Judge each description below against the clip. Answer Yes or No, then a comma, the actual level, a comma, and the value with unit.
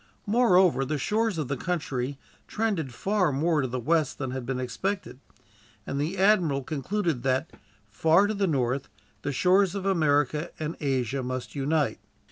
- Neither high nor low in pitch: Yes, medium, 155 Hz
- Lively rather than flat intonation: Yes, wide, 5.9 semitones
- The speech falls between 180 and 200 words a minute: No, average, 160 wpm